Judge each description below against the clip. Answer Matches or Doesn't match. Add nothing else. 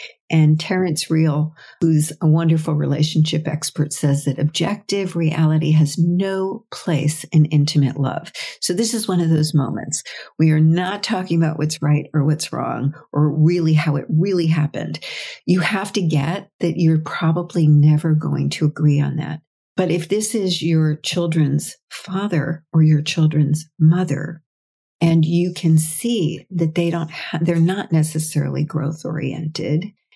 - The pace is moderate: Matches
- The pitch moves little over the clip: Matches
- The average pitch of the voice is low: Doesn't match